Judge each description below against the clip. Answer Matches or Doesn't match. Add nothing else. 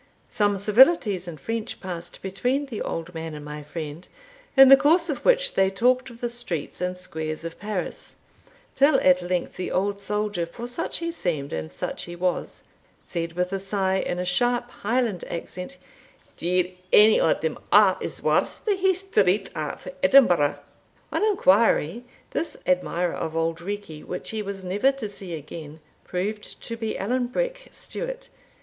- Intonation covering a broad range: Matches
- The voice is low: Doesn't match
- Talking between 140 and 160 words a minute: Doesn't match